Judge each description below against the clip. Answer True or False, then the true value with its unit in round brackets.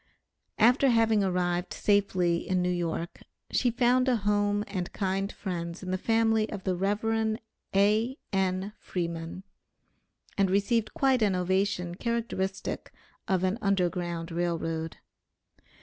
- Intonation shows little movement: False (3.5 semitones)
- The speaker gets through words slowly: True (125 wpm)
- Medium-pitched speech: False (195 Hz)